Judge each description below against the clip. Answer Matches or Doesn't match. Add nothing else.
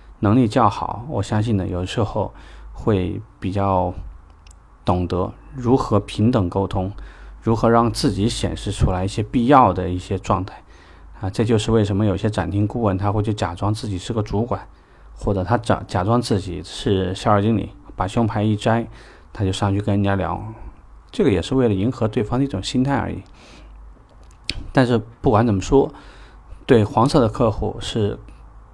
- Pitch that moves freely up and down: Doesn't match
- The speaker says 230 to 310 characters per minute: Matches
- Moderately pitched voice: Doesn't match